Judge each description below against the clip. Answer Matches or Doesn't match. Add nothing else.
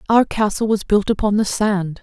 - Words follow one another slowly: Doesn't match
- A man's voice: Doesn't match